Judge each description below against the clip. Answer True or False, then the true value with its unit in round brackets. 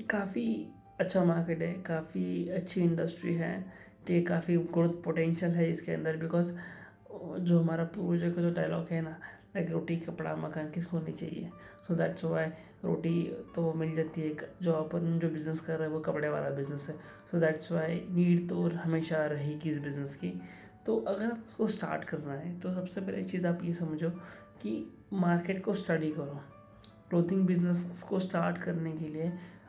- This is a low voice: False (165 Hz)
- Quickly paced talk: False (180 wpm)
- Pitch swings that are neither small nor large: False (1.8 semitones)